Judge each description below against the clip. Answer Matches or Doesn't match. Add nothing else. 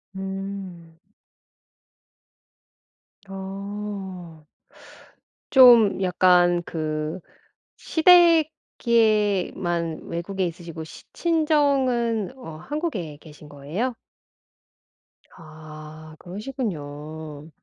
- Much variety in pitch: Matches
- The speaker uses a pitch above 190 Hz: Doesn't match